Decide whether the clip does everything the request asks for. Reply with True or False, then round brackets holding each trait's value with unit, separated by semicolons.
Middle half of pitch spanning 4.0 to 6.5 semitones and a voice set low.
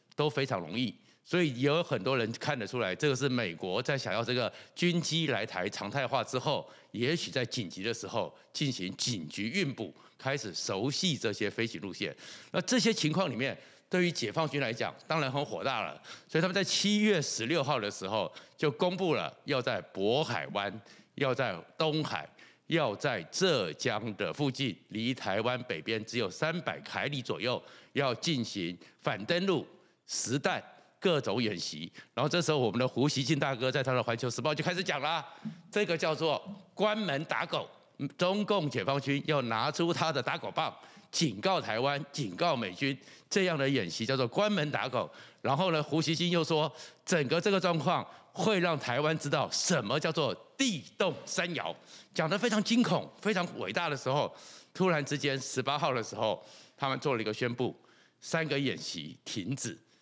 False (5.5 semitones; 145 Hz)